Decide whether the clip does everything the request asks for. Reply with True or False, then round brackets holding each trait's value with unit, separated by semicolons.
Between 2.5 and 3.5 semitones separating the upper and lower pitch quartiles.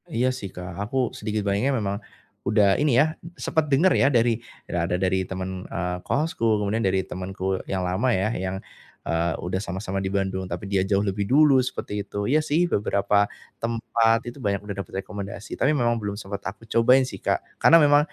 False (3.9 semitones)